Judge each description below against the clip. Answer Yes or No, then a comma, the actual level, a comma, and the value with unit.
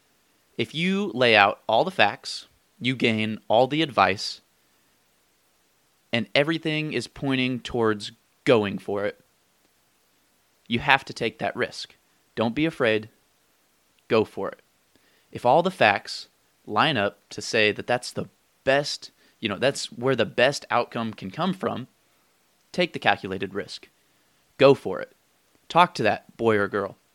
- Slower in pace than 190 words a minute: Yes, average, 150 wpm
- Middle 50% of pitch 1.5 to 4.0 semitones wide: No, average, 4.6 semitones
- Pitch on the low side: Yes, low, 125 Hz